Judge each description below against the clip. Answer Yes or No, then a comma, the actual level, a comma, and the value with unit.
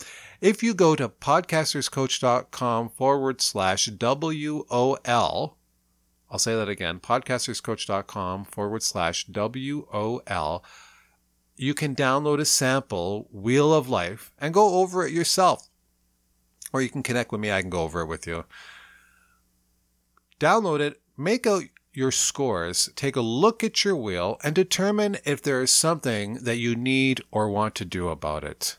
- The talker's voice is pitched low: Yes, low, 125 Hz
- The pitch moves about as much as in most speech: No, wide, 6.8 semitones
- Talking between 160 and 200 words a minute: No, average, 150 wpm